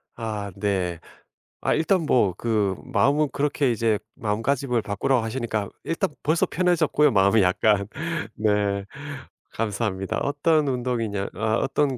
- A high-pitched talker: No, low, 115 Hz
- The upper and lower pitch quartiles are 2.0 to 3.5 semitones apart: No, average, 5.3 semitones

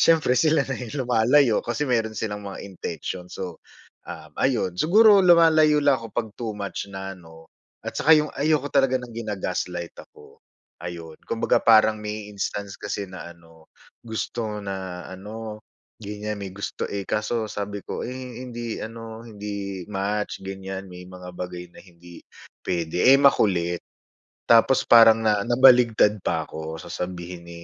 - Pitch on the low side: Yes, low, 105 Hz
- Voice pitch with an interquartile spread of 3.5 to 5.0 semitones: Yes, average, 4.5 semitones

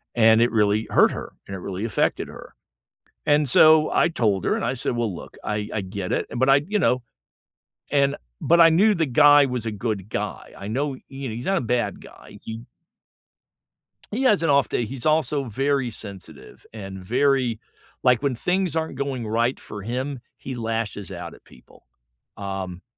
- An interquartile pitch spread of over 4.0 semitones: Yes, average, 5.2 semitones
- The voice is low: Yes, low, 120 Hz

